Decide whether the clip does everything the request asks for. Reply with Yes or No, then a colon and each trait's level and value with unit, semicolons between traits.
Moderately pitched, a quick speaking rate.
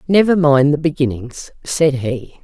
No: medium, 145 Hz; average, 150 wpm